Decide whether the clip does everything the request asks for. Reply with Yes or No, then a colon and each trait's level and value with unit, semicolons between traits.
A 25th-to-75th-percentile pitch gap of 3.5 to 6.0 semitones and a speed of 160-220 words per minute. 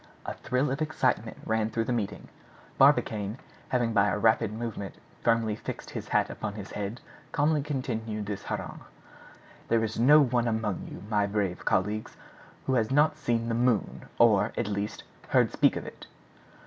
No: average, 3.0 semitones; average, 170 wpm